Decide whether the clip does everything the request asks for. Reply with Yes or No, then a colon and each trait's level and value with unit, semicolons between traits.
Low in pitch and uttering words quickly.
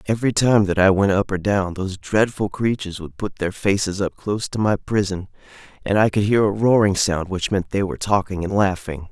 Yes: low, 100 Hz; fast, 225 wpm